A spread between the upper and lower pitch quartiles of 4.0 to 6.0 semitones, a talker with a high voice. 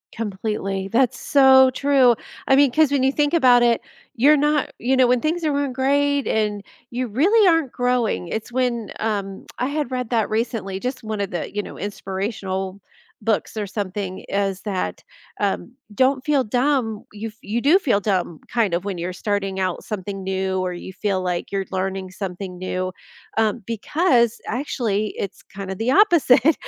Yes: average, 5.2 semitones; high, 220 Hz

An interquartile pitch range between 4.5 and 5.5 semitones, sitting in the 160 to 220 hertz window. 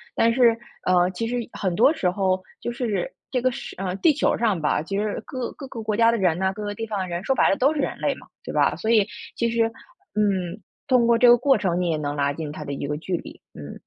Yes: average, 4.9 semitones; high, 210 Hz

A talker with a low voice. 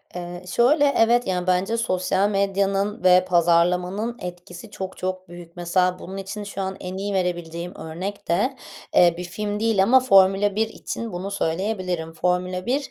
No: medium, 185 Hz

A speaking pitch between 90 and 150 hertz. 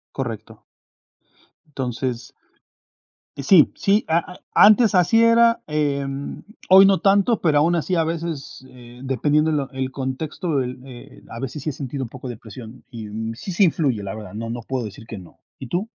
Yes: medium, 140 Hz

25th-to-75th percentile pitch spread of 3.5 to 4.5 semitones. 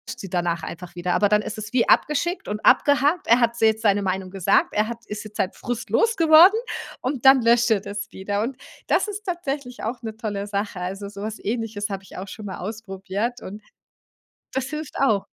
Yes: average, 4.2 semitones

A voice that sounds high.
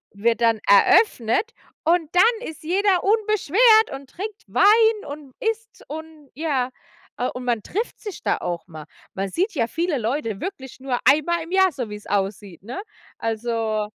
Yes: very high, 295 Hz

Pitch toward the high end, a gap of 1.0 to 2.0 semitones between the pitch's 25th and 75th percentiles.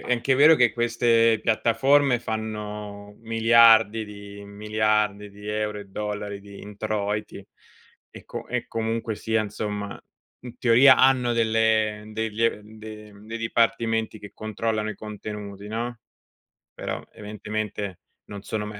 No: low, 110 Hz; narrow, 1.7 semitones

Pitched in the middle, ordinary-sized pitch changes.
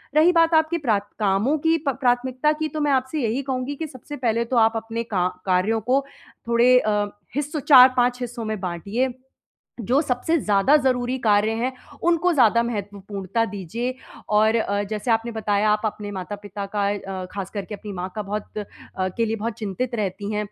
No: high, 230 Hz; average, 4.0 semitones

